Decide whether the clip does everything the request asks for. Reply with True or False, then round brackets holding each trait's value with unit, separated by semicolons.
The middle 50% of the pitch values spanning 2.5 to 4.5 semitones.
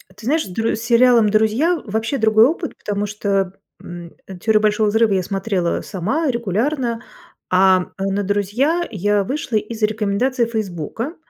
True (3.0 semitones)